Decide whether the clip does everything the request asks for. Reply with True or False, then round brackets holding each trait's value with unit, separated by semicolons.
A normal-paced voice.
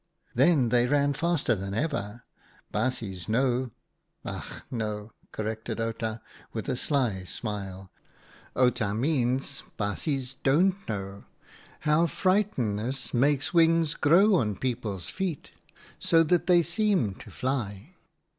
False (130 wpm)